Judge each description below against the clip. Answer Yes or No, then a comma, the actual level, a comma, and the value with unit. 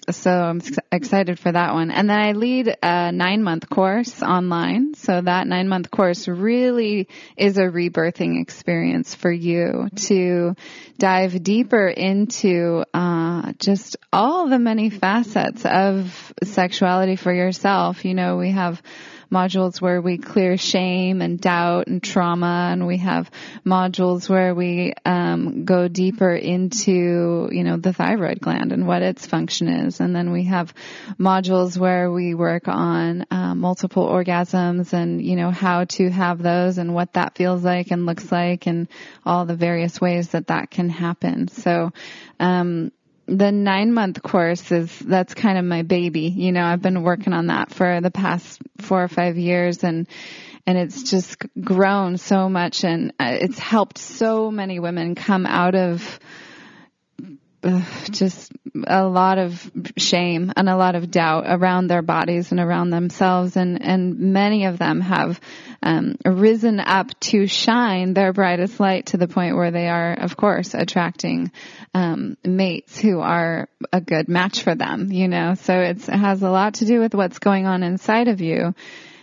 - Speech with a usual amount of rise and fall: No, narrow, 1.9 semitones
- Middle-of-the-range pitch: Yes, medium, 180 Hz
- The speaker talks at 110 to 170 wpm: Yes, average, 165 wpm